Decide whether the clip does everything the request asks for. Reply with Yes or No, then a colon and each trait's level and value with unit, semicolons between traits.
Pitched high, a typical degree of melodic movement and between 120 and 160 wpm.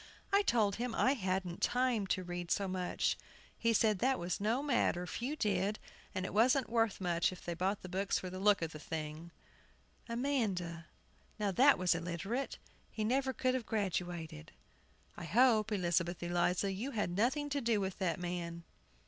No: high, 195 Hz; average, 4.9 semitones; average, 175 wpm